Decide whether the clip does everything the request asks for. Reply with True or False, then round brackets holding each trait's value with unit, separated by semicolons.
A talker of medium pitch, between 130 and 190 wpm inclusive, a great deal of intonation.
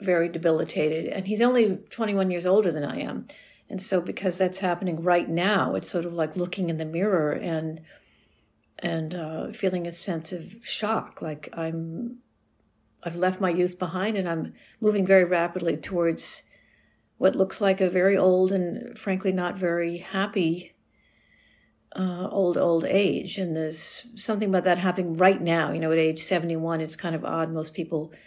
False (180 Hz; 170 wpm; 2.7 semitones)